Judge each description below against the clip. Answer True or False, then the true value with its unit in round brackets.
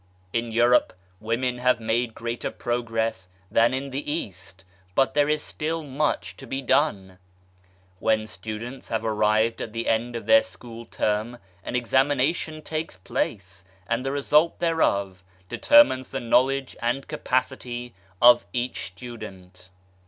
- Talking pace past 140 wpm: False (135 wpm)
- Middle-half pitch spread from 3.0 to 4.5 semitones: True (3.5 semitones)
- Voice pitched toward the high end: False (120 Hz)